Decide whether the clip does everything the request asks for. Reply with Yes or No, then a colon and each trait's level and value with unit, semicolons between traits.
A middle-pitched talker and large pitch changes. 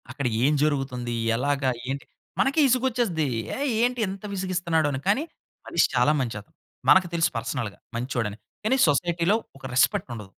Yes: medium, 155 Hz; wide, 7.3 semitones